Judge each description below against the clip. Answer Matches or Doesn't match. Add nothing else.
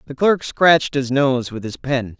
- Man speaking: Matches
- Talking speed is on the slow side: Doesn't match